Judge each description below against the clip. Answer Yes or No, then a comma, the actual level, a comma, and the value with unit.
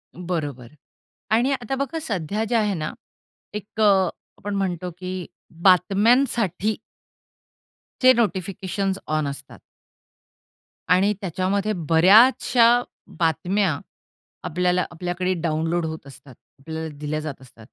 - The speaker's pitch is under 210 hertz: Yes, medium, 185 Hz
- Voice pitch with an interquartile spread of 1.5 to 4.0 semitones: No, average, 4.6 semitones